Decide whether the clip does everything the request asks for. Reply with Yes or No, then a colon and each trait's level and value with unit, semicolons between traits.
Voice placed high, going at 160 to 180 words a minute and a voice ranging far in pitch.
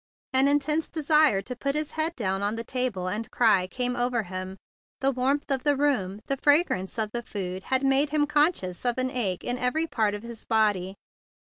No: very high, 250 Hz; fast, 205 wpm; wide, 5.8 semitones